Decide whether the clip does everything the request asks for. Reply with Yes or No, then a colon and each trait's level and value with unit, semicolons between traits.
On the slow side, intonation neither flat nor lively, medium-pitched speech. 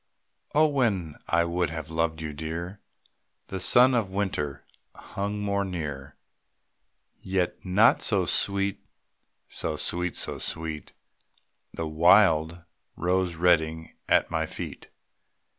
No: slow, 115 wpm; average, 3.5 semitones; very low, 90 Hz